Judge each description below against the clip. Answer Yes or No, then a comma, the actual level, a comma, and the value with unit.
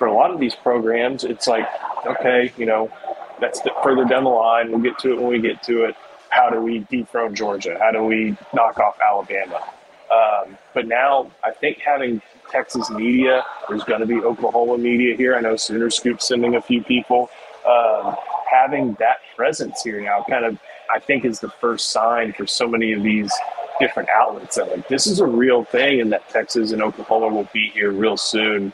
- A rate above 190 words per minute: Yes, fast, 205 wpm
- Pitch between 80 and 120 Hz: Yes, low, 115 Hz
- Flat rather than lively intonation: Yes, narrow, 1.9 semitones